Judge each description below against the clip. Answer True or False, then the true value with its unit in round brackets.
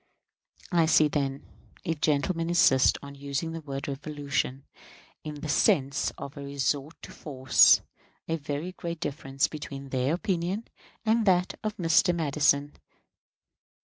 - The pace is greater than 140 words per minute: False (135 wpm)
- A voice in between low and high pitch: True (150 Hz)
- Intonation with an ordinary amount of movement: True (3.2 semitones)